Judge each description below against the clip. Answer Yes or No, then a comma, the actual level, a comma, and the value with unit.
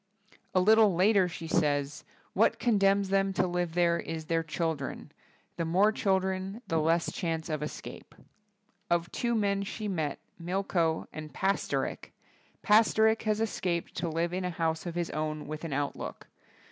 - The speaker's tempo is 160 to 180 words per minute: Yes, average, 165 wpm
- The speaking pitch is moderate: Yes, medium, 175 Hz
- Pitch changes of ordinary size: Yes, average, 3.3 semitones